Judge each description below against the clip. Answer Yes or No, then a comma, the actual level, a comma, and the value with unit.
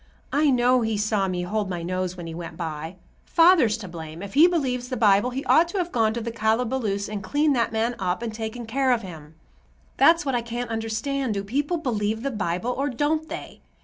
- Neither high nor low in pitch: No, high, 225 Hz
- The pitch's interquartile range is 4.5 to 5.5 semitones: Yes, average, 5.1 semitones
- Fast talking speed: Yes, fast, 220 wpm